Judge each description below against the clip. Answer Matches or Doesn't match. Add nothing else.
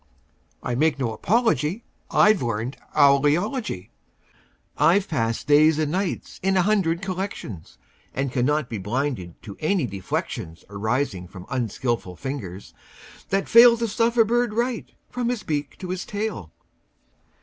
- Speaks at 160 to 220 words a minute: Doesn't match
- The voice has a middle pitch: Matches